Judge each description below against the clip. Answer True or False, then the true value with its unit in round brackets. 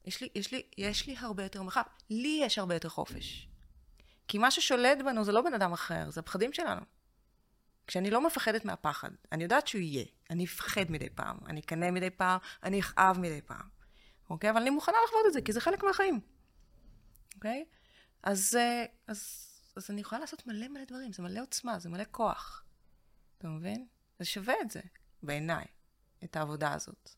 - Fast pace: True (185 wpm)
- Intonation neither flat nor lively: False (6.3 semitones)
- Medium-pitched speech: False (200 Hz)